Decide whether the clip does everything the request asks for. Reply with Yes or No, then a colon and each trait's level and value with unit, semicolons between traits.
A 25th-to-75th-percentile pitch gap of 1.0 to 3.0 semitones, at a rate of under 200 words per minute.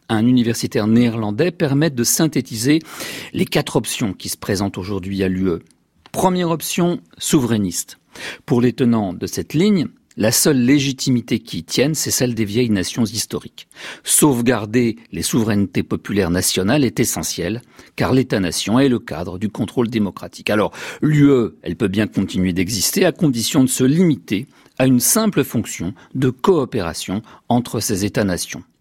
No: average, 4.9 semitones; average, 150 wpm